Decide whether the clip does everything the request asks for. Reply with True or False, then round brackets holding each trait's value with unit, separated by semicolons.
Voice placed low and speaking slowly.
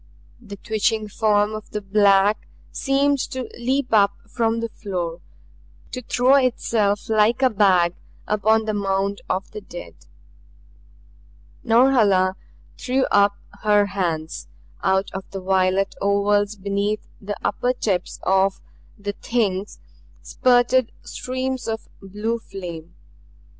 False (205 Hz; 120 wpm)